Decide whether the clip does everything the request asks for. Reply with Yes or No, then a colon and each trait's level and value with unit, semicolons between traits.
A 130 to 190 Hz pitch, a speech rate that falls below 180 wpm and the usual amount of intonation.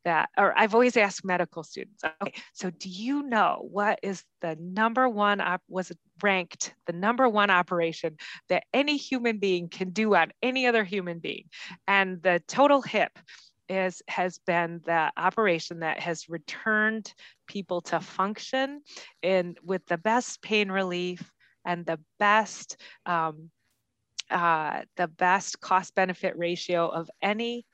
Yes: medium, 185 Hz; average, 145 wpm; average, 3.9 semitones